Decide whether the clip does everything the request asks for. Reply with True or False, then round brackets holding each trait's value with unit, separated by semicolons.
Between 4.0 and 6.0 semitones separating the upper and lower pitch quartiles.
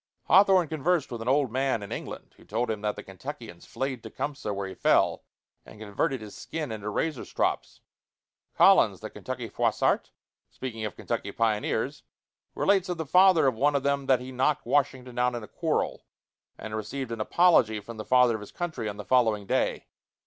True (5.1 semitones)